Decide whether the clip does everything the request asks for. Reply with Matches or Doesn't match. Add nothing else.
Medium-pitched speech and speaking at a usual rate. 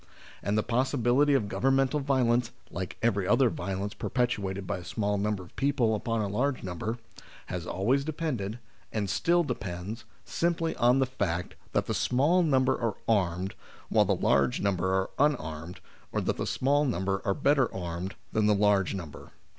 Doesn't match